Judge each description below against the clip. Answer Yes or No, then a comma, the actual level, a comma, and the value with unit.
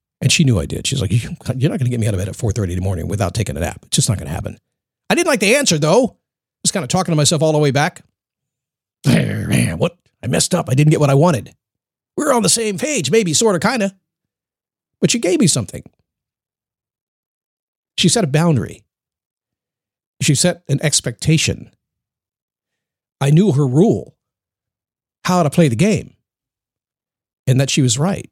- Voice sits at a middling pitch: Yes, medium, 145 Hz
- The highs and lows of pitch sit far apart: Yes, wide, 6.6 semitones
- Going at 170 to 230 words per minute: Yes, average, 200 wpm